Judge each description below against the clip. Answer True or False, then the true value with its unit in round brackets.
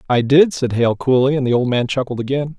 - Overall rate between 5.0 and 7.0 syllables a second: True (5.8 syllables/s)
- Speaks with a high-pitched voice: False (130 Hz)